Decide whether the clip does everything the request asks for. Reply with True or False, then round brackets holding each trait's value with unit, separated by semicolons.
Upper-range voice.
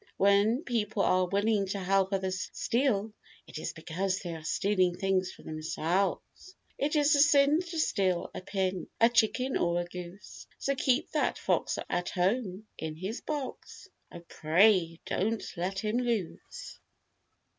True (195 Hz)